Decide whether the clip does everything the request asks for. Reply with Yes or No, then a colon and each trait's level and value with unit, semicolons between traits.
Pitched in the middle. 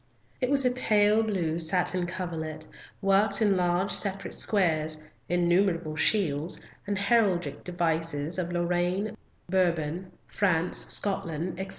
Yes: medium, 180 Hz